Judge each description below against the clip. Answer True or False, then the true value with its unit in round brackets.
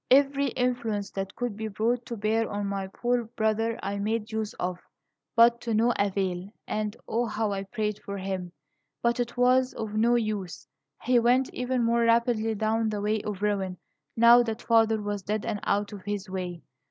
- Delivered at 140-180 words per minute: False (190 wpm)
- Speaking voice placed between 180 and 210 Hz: False (220 Hz)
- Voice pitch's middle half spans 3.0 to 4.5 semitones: False (2.6 semitones)